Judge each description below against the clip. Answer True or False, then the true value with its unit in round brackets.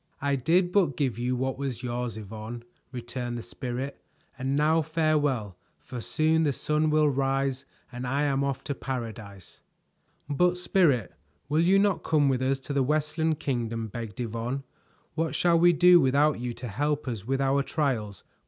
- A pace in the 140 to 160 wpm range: False (170 wpm)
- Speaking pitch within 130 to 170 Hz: True (135 Hz)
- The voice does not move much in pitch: False (3.9 semitones)